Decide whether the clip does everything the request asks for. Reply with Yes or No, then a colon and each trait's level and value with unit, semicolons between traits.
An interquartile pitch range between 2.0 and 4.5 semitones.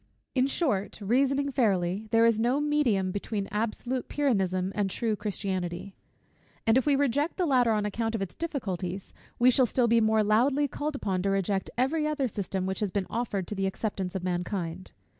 No: average, 5.3 semitones